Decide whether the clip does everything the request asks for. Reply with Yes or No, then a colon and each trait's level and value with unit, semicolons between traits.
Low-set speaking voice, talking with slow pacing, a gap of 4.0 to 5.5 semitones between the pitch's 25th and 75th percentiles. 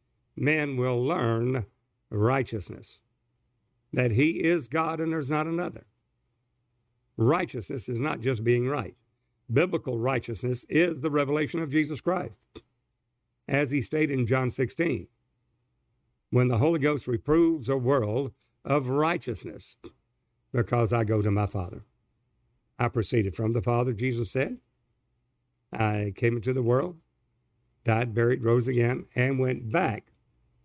No: low, 125 Hz; slow, 130 wpm; average, 2.7 semitones